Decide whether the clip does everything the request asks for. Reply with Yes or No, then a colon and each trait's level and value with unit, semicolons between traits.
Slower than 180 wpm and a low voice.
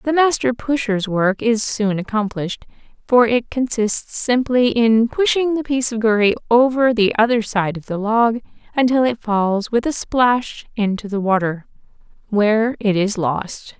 No: average, 160 wpm; high, 225 Hz